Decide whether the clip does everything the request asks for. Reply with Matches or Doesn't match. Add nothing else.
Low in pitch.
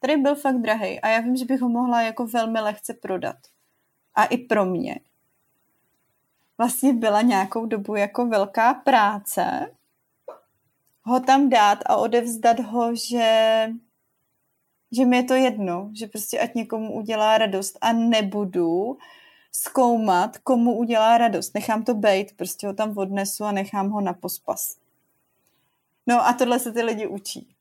Doesn't match